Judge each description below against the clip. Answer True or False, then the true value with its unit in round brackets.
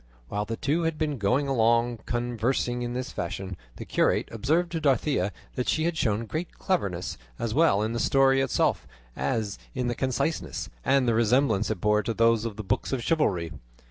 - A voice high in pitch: False (120 Hz)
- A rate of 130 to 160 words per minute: False (190 wpm)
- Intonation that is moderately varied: True (4.3 semitones)